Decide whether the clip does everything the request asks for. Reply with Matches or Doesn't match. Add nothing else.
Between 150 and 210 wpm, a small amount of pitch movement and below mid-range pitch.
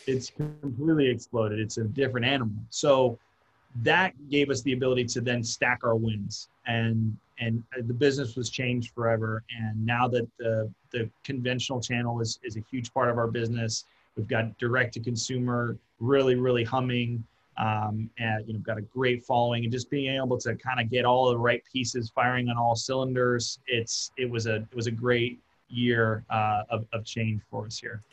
Matches